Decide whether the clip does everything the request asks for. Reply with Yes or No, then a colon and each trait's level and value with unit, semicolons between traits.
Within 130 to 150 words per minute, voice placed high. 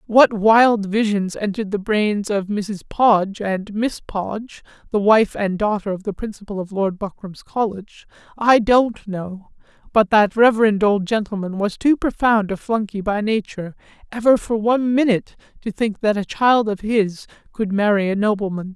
No: average, 170 wpm; high, 210 Hz